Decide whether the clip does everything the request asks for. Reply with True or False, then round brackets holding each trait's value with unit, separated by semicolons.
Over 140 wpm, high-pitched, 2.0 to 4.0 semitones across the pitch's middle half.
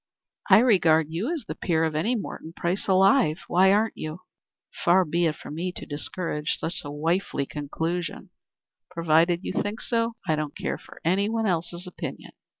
False (175 wpm; 175 Hz; 3.4 semitones)